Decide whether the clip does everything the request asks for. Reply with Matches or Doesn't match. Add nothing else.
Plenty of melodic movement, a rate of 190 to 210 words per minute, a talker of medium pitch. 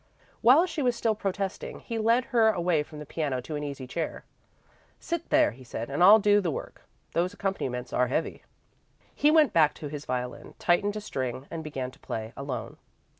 Matches